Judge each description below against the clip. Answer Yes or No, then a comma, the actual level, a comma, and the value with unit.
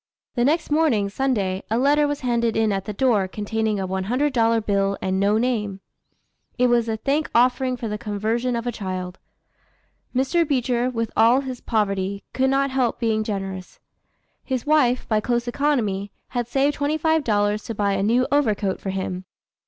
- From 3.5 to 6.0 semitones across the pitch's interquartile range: Yes, average, 4.2 semitones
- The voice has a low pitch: No, high, 230 Hz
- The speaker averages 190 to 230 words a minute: No, average, 175 wpm